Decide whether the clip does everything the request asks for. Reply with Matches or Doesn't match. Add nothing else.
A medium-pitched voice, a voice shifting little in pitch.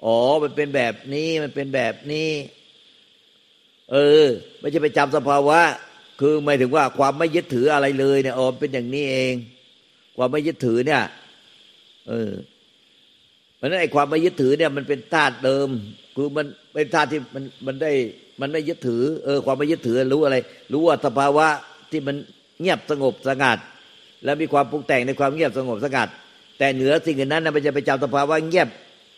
Matches